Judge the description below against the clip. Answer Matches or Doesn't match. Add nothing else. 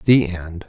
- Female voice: Doesn't match